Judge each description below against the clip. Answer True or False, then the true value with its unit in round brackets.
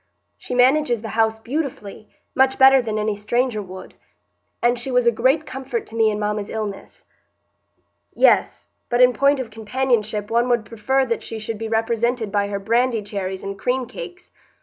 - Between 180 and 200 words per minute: False (170 wpm)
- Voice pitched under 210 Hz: False (230 Hz)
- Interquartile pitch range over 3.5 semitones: False (3.2 semitones)